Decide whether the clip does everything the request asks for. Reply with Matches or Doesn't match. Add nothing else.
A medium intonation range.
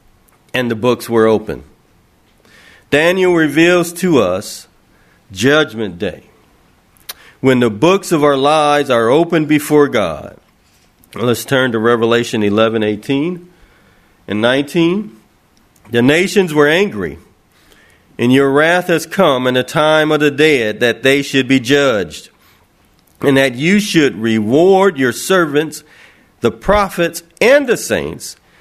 Doesn't match